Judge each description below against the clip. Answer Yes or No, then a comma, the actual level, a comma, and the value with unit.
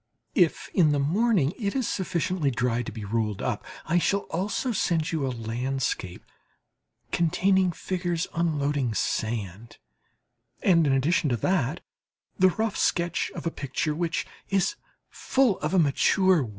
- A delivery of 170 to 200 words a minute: No, average, 150 wpm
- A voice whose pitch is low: No, medium, 165 Hz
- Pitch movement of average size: No, wide, 5.8 semitones